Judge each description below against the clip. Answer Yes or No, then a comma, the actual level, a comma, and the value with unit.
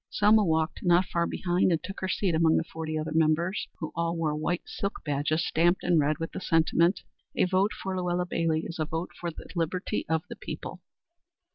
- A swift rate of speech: Yes, fast, 210 wpm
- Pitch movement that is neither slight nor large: No, narrow, 2.1 semitones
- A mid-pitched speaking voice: Yes, medium, 170 Hz